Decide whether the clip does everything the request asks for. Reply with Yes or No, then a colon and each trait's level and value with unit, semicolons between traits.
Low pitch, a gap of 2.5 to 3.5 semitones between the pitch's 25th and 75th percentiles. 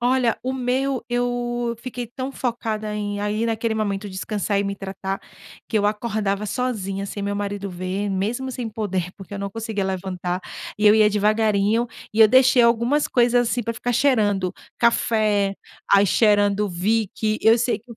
No: high, 215 Hz; average, 3.1 semitones